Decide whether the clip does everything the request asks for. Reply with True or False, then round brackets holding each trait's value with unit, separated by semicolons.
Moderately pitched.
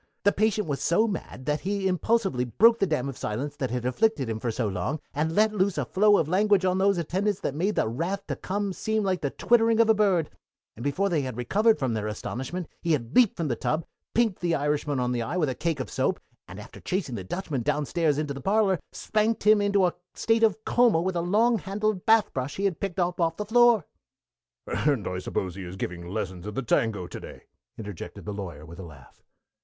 True (170 Hz)